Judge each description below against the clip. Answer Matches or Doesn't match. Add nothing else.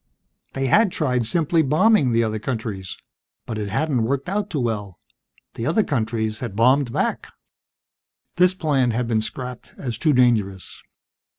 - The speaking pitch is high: Doesn't match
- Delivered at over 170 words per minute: Doesn't match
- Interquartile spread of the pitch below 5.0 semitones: Doesn't match